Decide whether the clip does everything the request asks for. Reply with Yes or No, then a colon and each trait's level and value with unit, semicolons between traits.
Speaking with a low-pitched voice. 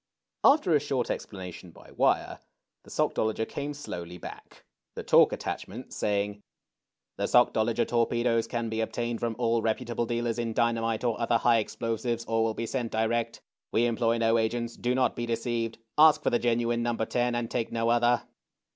Yes: low, 115 Hz